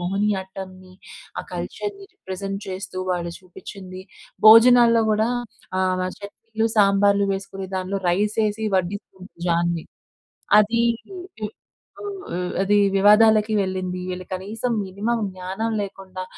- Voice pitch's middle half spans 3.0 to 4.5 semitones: No, narrow, 2.5 semitones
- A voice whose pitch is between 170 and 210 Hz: Yes, high, 195 Hz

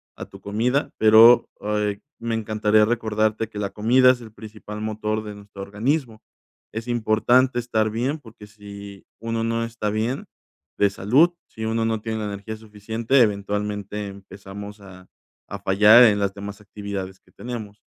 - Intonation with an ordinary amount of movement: No, narrow, 2.0 semitones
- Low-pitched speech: Yes, low, 110 Hz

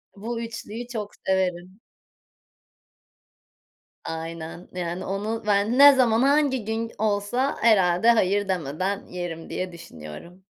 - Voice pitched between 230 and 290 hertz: No, high, 200 Hz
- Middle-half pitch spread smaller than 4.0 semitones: No, average, 4.3 semitones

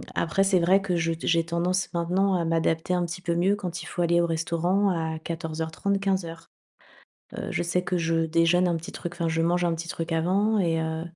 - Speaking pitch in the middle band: Yes, medium, 170 Hz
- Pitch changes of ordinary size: No, narrow, 1.8 semitones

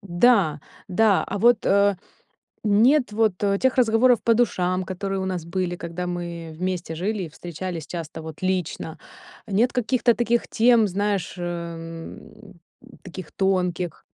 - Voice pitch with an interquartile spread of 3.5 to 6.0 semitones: Yes, average, 4.1 semitones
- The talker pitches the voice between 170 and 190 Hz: Yes, medium, 185 Hz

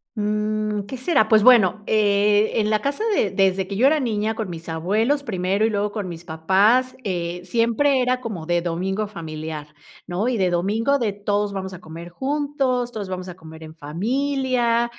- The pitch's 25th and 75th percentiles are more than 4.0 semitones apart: Yes, average, 4.7 semitones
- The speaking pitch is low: No, high, 210 Hz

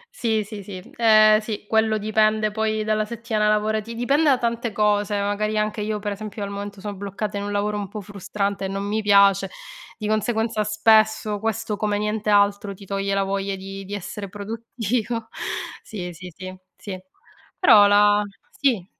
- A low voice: No, high, 210 Hz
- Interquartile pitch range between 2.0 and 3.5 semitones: No, narrow, 1.4 semitones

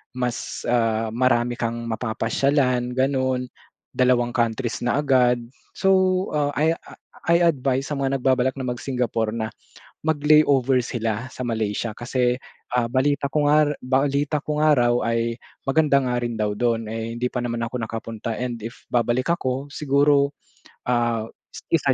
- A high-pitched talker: No, low, 125 Hz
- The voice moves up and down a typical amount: Yes, average, 3.1 semitones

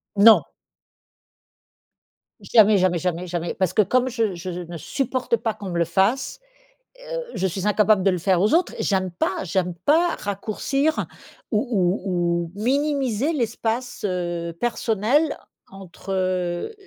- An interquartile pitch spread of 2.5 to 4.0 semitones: No, average, 4.7 semitones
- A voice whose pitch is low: No, high, 195 Hz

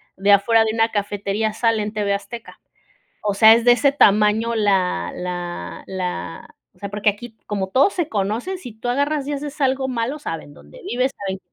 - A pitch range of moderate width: Yes, average, 3.5 semitones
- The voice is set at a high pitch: Yes, high, 215 Hz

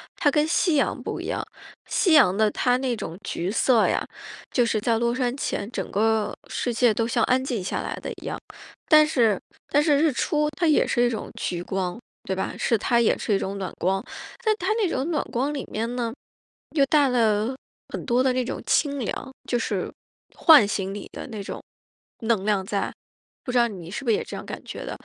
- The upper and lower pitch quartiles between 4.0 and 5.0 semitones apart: Yes, average, 4.7 semitones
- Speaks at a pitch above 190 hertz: Yes, high, 235 Hz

